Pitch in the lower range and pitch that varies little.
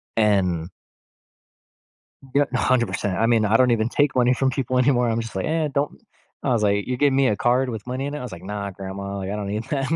No: low, 120 Hz; average, 4.2 semitones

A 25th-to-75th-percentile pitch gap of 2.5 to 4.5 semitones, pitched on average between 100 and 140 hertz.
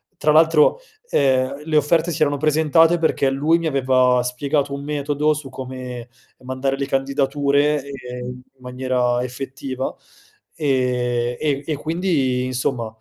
Yes: average, 2.9 semitones; low, 135 Hz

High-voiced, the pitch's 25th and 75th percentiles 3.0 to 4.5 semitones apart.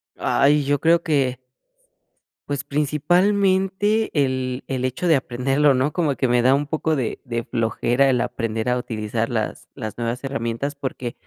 No: low, 135 Hz; average, 3.6 semitones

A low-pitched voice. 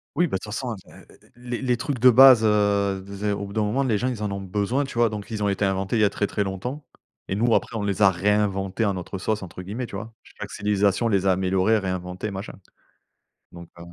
Yes: low, 105 Hz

